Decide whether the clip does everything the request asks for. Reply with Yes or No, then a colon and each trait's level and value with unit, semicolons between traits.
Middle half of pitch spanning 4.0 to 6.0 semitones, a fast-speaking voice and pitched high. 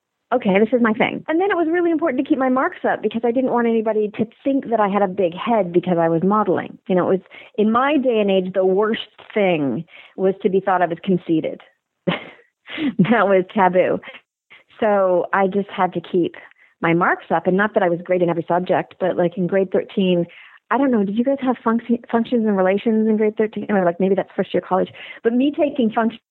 Yes: average, 4.5 semitones; fast, 235 wpm; high, 210 Hz